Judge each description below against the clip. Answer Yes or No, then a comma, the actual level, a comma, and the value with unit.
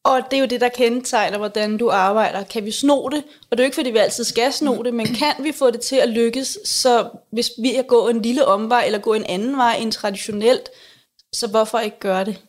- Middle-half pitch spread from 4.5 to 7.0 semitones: No, average, 3.1 semitones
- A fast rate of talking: Yes, fast, 255 wpm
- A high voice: Yes, high, 235 Hz